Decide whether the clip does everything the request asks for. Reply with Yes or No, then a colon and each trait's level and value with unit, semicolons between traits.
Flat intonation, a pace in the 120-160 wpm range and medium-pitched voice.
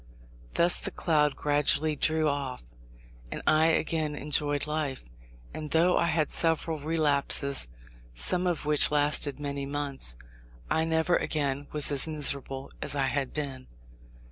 Yes: narrow, 2.0 semitones; average, 140 wpm; medium, 150 Hz